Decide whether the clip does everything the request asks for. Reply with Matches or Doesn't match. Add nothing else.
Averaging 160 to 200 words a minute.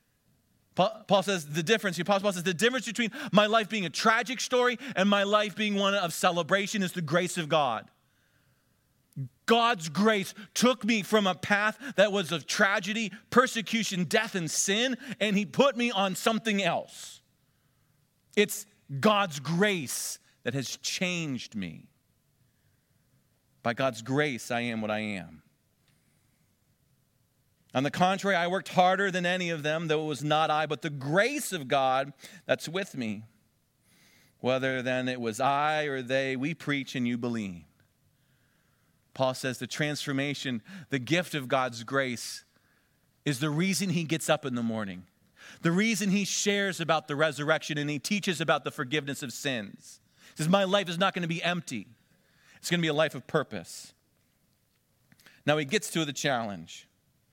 Matches